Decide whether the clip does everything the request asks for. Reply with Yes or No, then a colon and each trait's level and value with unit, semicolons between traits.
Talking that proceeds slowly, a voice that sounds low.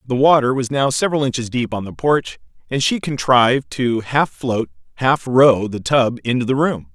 No: average, 200 wpm; low, 125 Hz